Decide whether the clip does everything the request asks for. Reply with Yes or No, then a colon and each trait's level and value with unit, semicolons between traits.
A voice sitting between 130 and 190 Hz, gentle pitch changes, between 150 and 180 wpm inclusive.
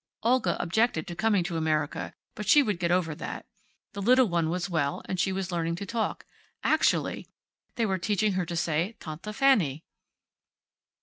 No: medium, 185 Hz; average, 4.2 semitones; average, 175 wpm